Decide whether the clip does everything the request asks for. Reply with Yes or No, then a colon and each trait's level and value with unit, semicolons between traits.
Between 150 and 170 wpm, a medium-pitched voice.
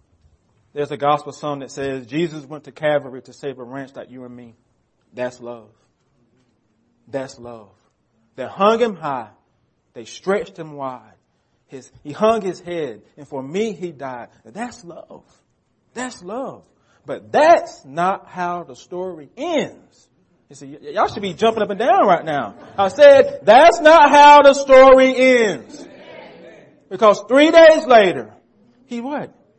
Yes: average, 155 wpm; medium, 155 Hz